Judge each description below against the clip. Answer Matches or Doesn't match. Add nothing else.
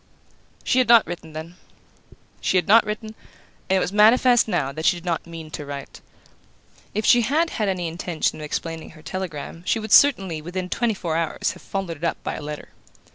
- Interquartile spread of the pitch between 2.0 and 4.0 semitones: Doesn't match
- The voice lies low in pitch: Doesn't match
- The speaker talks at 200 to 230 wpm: Matches